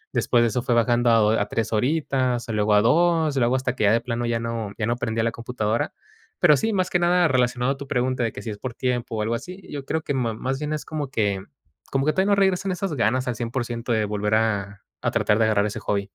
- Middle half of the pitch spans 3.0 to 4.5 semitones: Yes, average, 3.8 semitones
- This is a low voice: Yes, low, 120 Hz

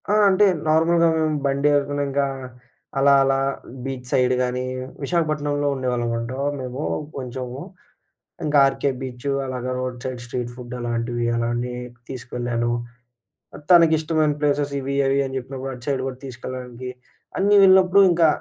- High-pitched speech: No, low, 135 Hz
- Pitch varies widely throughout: No, average, 2.7 semitones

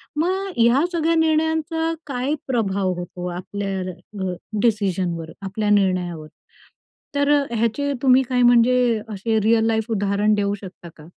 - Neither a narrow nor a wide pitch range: No, wide, 5.7 semitones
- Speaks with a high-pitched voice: Yes, high, 220 Hz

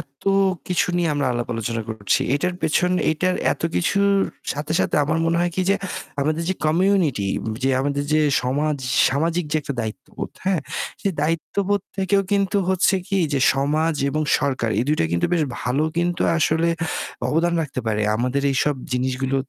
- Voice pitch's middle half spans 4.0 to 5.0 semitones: Yes, average, 4.6 semitones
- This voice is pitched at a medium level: Yes, medium, 155 Hz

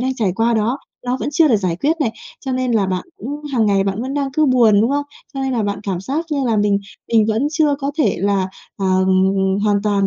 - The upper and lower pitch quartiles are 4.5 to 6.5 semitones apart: Yes, average, 5.1 semitones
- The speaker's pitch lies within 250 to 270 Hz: No, high, 230 Hz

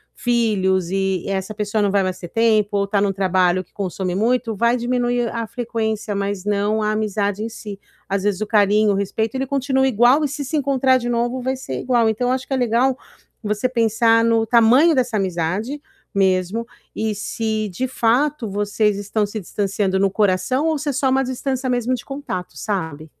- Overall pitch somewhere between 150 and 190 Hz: No, high, 220 Hz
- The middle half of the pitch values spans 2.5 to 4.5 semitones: Yes, average, 3.8 semitones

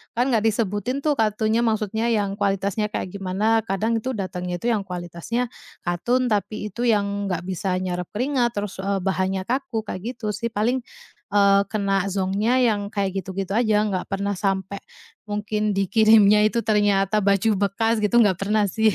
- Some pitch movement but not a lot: No, narrow, 2.3 semitones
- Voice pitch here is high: Yes, high, 205 Hz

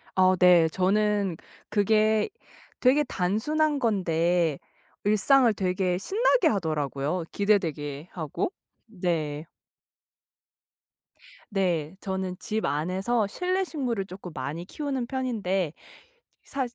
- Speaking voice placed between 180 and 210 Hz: Yes, high, 190 Hz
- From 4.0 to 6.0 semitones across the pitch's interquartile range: Yes, average, 5.2 semitones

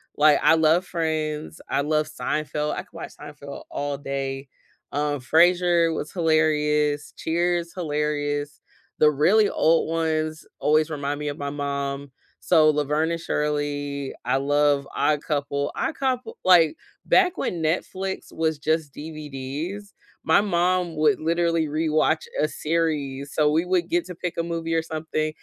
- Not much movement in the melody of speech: Yes, narrow, 2.3 semitones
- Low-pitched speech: No, medium, 155 Hz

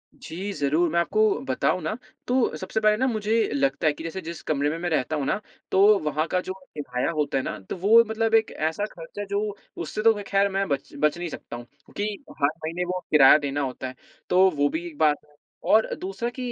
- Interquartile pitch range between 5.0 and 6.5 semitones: Yes, wide, 5.5 semitones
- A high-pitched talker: No, medium, 170 Hz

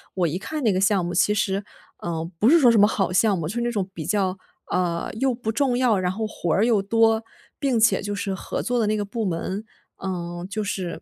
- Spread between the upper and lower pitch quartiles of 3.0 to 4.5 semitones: Yes, average, 3.5 semitones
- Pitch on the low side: No, high, 205 Hz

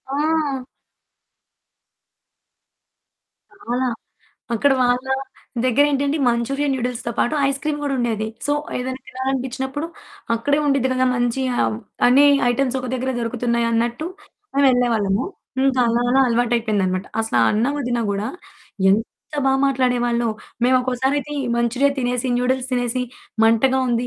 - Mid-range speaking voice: No, very high, 250 Hz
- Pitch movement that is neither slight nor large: No, narrow, 2.3 semitones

